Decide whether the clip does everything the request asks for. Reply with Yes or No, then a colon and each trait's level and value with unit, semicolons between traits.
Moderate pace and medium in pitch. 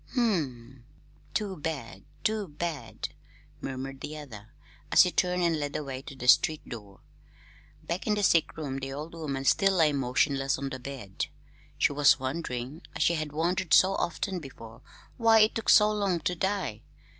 Yes: average, 180 wpm; medium, 150 Hz